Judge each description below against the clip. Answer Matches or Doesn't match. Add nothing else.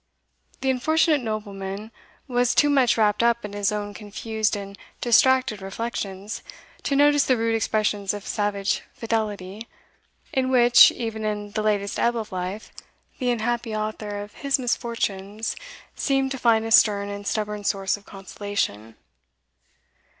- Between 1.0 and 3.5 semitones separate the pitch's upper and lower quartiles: Matches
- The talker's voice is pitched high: Matches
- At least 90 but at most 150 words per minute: Matches